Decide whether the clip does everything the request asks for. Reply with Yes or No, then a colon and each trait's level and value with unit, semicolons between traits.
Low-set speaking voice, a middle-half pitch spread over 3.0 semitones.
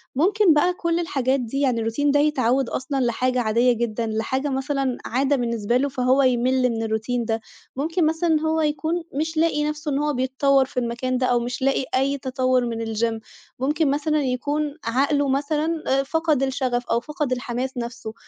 No: very high, 265 Hz; average, 3.4 semitones